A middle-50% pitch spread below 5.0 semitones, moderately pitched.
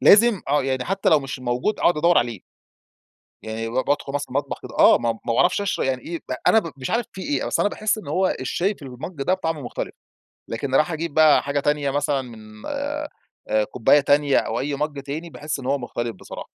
Yes: average, 4.6 semitones; medium, 145 Hz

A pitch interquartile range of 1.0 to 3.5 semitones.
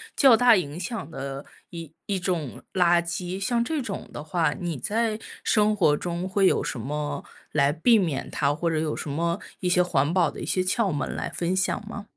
No: average, 4.7 semitones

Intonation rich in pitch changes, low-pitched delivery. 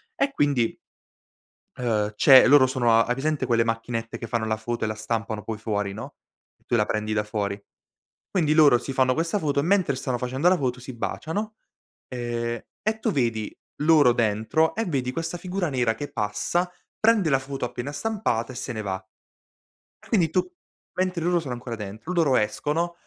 Yes: wide, 5.9 semitones; low, 125 Hz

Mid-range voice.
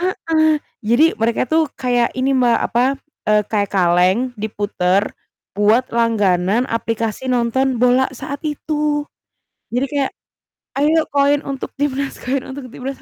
No: very high, 250 Hz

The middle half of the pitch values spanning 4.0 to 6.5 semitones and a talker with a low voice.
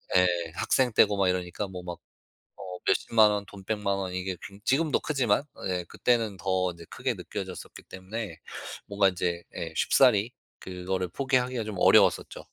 No: average, 3.3 semitones; low, 100 Hz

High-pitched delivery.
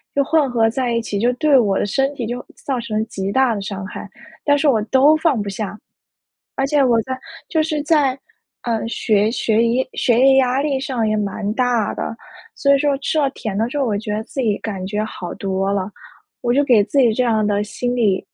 Yes: high, 235 Hz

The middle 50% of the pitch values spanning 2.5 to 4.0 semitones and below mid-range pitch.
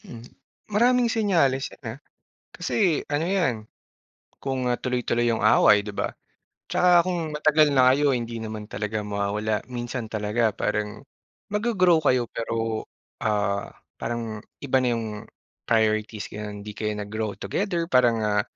No: average, 4.8 semitones; low, 115 Hz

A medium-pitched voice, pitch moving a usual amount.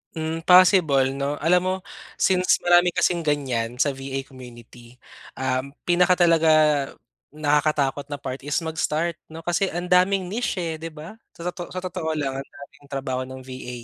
Yes: medium, 150 Hz; average, 4.5 semitones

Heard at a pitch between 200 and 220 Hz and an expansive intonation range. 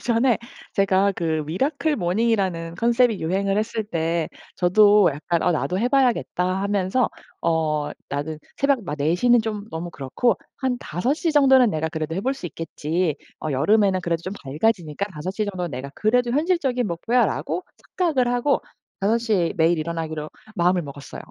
No: high, 190 Hz; wide, 6.2 semitones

